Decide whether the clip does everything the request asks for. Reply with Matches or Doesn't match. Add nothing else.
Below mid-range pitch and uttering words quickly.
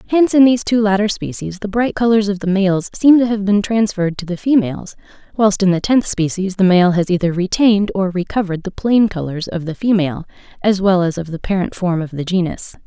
Doesn't match